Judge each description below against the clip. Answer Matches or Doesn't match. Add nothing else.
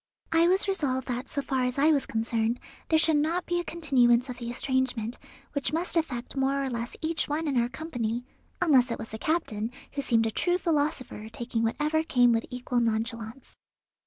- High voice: Matches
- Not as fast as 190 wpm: Doesn't match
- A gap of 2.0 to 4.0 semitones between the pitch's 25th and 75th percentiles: Doesn't match